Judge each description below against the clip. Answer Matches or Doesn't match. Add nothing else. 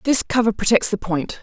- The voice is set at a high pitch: Matches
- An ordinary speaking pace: Doesn't match